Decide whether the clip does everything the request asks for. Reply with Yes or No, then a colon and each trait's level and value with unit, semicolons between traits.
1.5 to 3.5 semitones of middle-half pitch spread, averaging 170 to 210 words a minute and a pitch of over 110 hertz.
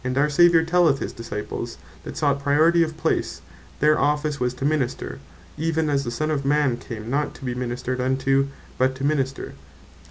Yes: average, 3.0 semitones; average, 180 wpm; medium, 140 Hz